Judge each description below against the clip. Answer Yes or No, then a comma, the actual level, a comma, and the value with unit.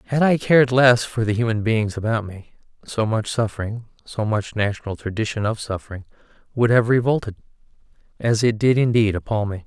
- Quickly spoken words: No, average, 175 wpm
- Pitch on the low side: Yes, low, 110 Hz